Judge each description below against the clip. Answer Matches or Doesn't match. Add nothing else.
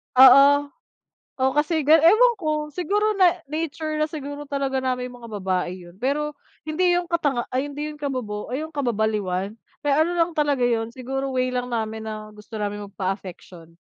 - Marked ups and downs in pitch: Matches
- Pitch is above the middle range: Matches